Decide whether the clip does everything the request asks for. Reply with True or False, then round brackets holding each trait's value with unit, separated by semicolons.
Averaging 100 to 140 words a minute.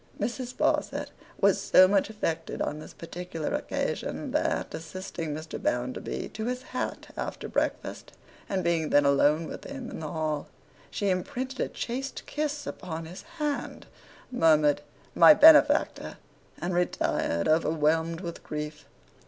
True (135 wpm)